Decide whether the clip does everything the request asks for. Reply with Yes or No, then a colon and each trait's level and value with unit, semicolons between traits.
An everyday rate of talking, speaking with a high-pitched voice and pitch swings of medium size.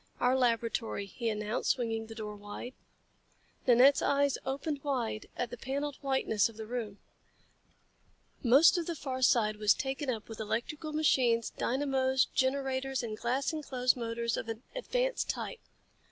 Yes: average, 150 wpm; very high, 250 Hz; average, 3.3 semitones